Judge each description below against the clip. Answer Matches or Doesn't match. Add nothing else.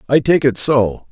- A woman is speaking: Doesn't match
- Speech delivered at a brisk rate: Matches